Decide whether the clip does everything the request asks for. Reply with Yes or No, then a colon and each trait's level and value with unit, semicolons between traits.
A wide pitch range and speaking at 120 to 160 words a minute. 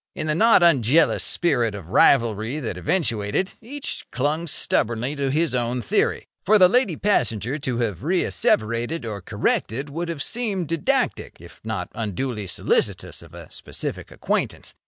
Yes: wide, 7.0 semitones; average, 150 wpm